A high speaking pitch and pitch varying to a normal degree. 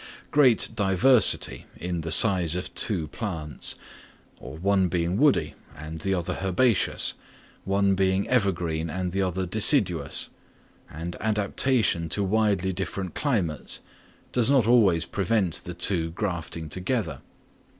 No: very low, 95 Hz; average, 3.8 semitones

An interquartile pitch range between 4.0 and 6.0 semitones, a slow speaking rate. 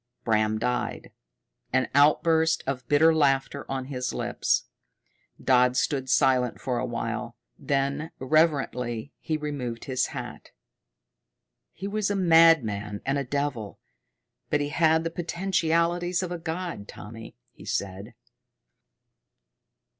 Yes: average, 4.6 semitones; slow, 120 wpm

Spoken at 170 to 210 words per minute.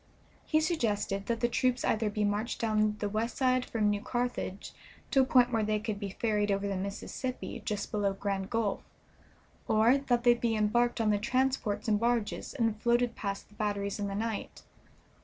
Yes: average, 190 wpm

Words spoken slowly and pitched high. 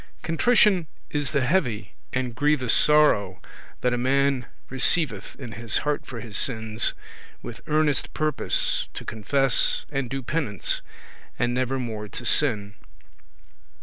No: slow, 130 wpm; low, 130 Hz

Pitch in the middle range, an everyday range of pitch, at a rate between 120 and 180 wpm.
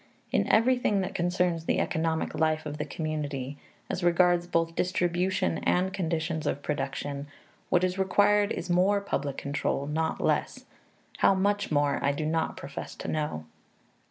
Yes: medium, 165 Hz; average, 3.6 semitones; average, 155 wpm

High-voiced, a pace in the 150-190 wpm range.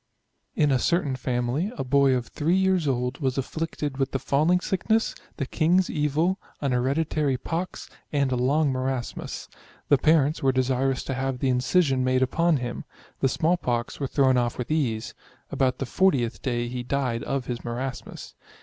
No: low, 135 Hz; average, 175 wpm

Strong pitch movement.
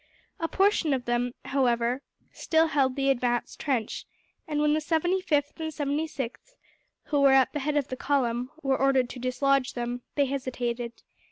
No: average, 3.2 semitones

